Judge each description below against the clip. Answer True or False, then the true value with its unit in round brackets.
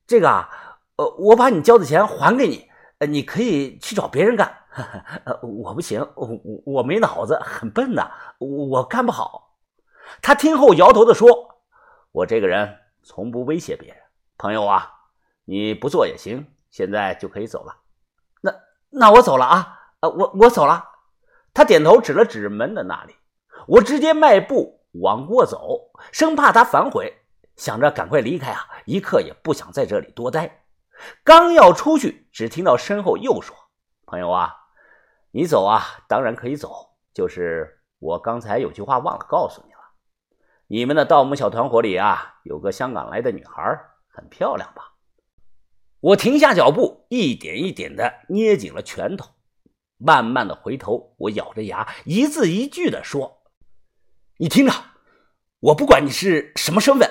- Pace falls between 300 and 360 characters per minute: False (235 characters per minute)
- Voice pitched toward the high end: True (305 Hz)